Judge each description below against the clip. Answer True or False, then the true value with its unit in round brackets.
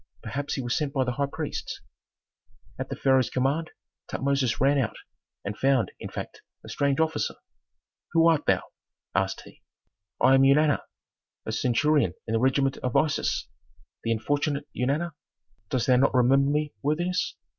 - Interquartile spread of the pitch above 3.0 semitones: False (2.6 semitones)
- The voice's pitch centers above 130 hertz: True (140 Hz)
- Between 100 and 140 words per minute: False (155 wpm)